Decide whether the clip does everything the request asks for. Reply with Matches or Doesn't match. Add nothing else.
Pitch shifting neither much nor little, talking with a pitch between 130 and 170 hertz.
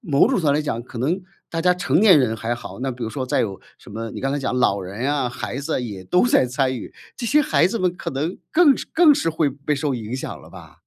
Doesn't match